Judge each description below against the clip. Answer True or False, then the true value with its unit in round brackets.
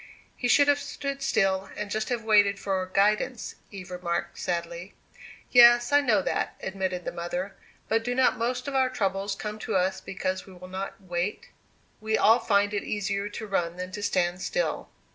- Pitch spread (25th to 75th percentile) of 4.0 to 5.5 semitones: False (3.4 semitones)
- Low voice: False (200 Hz)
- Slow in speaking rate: False (185 wpm)